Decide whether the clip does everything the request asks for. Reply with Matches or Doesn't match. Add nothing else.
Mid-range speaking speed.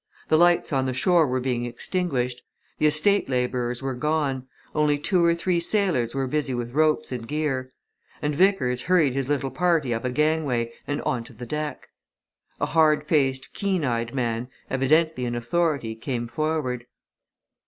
Matches